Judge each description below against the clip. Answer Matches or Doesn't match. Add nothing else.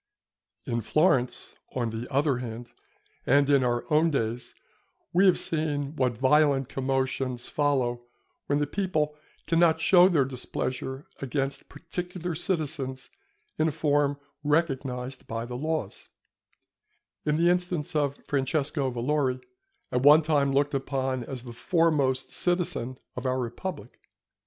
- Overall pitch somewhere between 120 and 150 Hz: Matches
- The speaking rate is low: Matches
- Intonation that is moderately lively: Matches